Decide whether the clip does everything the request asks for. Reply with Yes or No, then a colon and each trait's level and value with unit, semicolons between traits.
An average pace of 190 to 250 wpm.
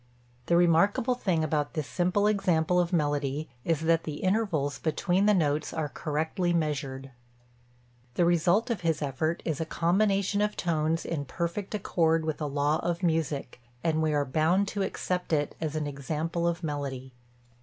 No: average, 165 wpm